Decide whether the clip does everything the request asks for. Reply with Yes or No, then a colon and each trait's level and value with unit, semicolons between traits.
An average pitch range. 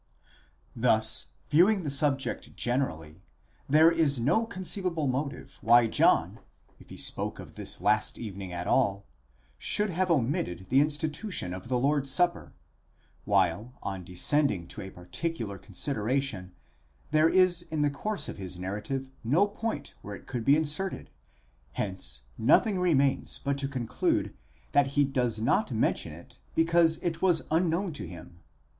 No: wide, 7.5 semitones